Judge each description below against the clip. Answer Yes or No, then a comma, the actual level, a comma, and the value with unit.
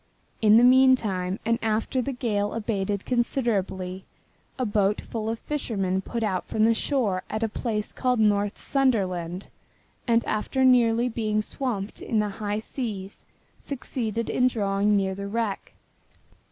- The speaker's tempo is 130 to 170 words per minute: Yes, average, 150 wpm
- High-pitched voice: Yes, high, 215 Hz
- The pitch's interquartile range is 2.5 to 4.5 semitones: Yes, average, 3.1 semitones